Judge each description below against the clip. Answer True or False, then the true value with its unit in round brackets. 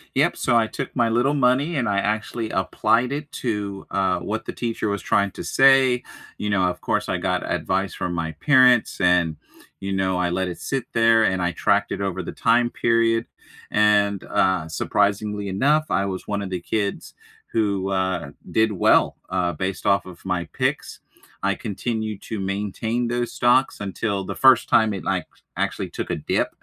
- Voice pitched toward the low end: True (105 Hz)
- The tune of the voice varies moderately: True (3.8 semitones)